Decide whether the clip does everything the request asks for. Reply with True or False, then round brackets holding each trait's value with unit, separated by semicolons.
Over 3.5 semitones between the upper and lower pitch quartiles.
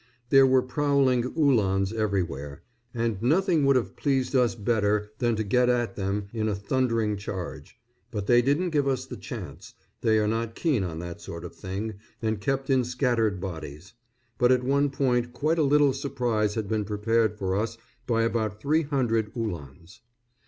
True (4.3 semitones)